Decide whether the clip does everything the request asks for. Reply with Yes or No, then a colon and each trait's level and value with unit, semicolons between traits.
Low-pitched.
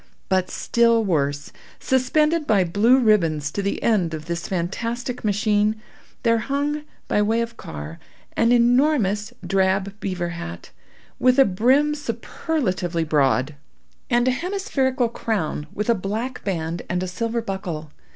No: high, 210 Hz